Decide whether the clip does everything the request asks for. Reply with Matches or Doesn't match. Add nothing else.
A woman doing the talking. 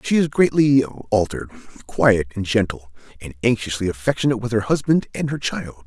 Doesn't match